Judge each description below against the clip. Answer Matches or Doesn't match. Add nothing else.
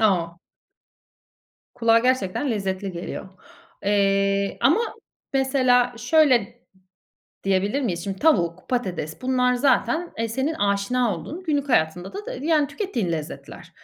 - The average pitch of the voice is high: Matches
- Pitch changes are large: Matches